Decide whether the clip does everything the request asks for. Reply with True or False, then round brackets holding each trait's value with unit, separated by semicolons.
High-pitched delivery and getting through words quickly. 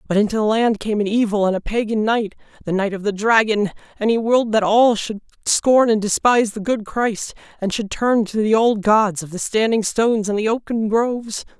True (215 Hz; 225 wpm)